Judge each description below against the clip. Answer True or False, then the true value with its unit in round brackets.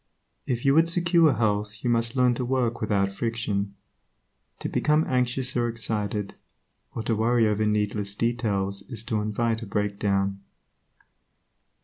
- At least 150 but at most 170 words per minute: False (140 wpm)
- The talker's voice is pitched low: True (115 Hz)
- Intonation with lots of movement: False (2.9 semitones)